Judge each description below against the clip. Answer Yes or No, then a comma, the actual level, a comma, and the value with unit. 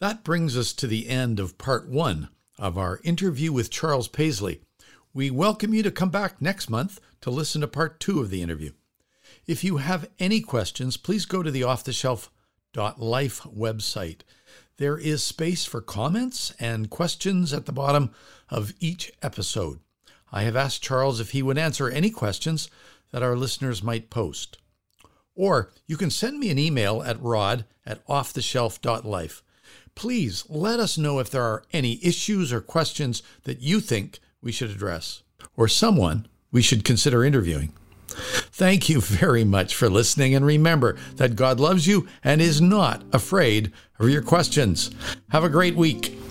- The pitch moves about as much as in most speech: No, wide, 6.4 semitones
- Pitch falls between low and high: No, low, 130 Hz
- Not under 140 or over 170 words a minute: Yes, average, 165 wpm